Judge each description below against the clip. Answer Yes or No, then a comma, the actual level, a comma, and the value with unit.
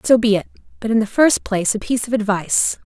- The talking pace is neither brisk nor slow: No, fast, 245 wpm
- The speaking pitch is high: Yes, high, 220 Hz